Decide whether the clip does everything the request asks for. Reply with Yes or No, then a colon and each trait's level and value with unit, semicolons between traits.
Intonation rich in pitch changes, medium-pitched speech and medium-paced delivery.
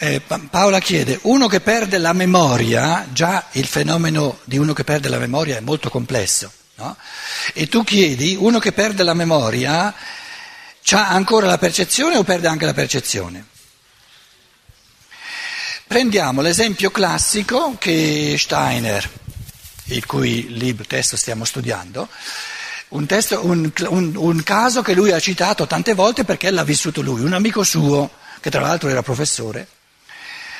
Yes: wide, 7.4 semitones; medium, 165 Hz; average, 140 wpm